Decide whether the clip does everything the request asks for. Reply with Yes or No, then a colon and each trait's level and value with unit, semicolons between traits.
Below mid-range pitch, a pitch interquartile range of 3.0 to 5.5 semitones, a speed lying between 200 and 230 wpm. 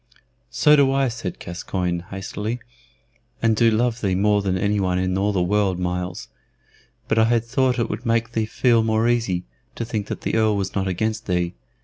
Yes: low, 105 Hz; average, 3.7 semitones; fast, 205 wpm